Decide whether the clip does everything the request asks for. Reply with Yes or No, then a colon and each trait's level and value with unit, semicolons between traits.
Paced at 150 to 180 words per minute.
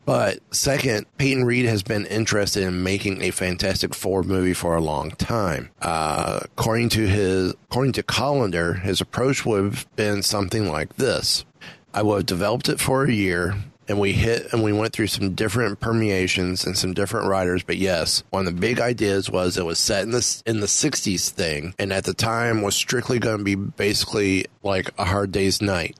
No: average, 200 wpm